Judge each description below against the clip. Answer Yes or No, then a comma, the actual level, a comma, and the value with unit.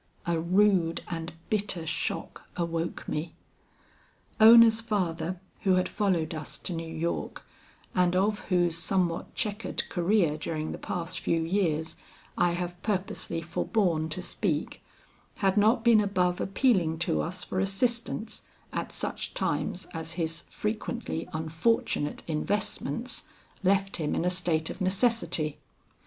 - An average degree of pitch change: Yes, average, 3.8 semitones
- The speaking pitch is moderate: Yes, medium, 180 Hz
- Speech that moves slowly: Yes, slow, 130 wpm